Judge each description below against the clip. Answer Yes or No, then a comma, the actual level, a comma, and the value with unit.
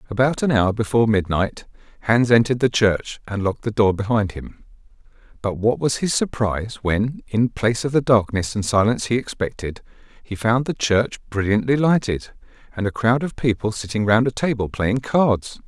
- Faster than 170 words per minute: Yes, average, 180 wpm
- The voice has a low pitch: Yes, low, 115 Hz